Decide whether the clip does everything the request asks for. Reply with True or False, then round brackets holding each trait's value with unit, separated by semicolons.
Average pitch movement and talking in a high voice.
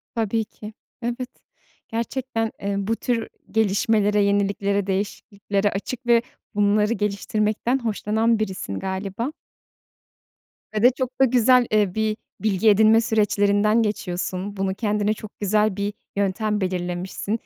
False (2.0 semitones; 210 Hz)